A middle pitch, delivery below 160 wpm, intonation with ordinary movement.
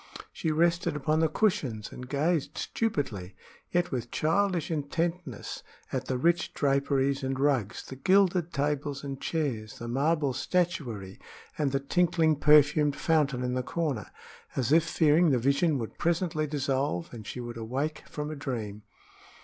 Yes: medium, 145 Hz; average, 150 wpm; average, 3.9 semitones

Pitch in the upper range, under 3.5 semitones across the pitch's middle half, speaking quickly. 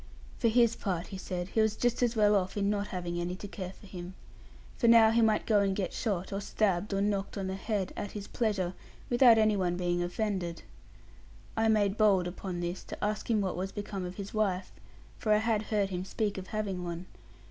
Yes: high, 200 Hz; average, 2.8 semitones; fast, 225 wpm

